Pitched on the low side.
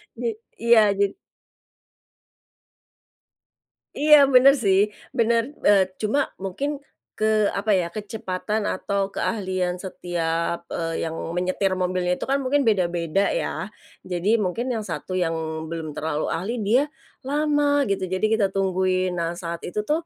No: high, 195 Hz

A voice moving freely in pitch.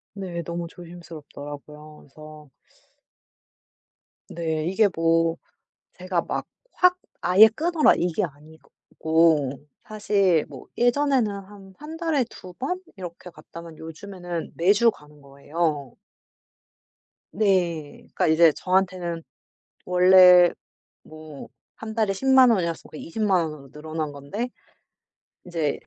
No: average, 4.2 semitones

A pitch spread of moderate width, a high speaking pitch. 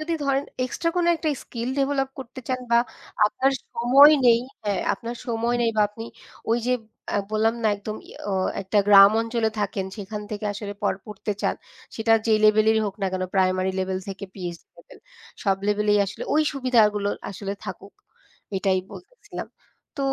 Yes: average, 3.4 semitones; high, 215 Hz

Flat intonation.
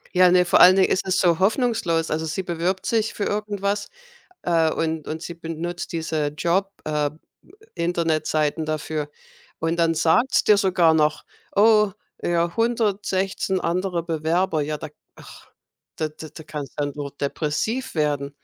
No: average, 3.5 semitones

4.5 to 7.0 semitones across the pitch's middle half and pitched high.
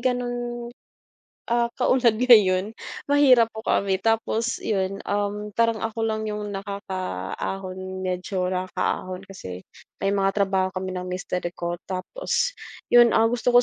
No: average, 3.7 semitones; high, 200 Hz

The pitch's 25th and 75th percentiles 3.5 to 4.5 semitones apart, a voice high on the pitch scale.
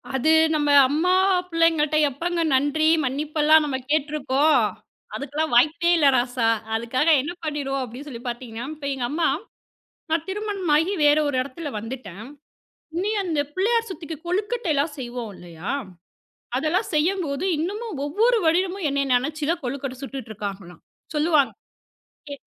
Yes: average, 4.2 semitones; very high, 295 Hz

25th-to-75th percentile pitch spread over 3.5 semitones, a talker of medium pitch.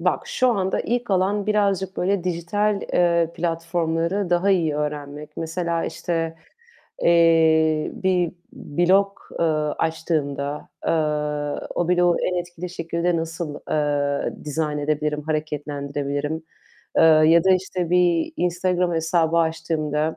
No: average, 2.7 semitones; medium, 165 Hz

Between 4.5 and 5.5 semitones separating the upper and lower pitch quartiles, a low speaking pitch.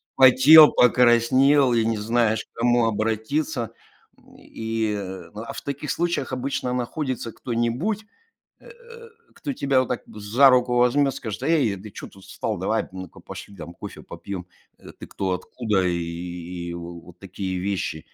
Yes: average, 5.1 semitones; low, 115 Hz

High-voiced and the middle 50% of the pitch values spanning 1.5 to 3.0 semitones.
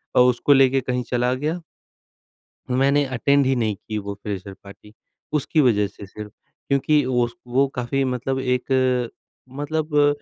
No: low, 130 Hz; average, 2.7 semitones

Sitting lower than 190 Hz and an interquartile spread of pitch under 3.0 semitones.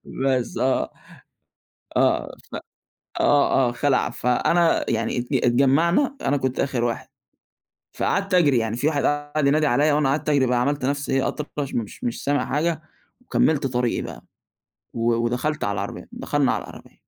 No: medium, 140 Hz; average, 3.4 semitones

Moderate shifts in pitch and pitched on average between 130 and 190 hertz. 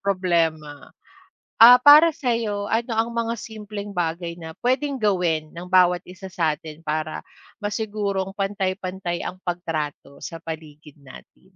Yes: average, 4.6 semitones; medium, 185 Hz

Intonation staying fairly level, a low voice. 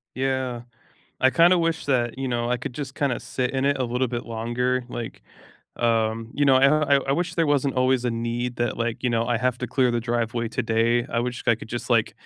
Yes: narrow, 2.1 semitones; low, 125 Hz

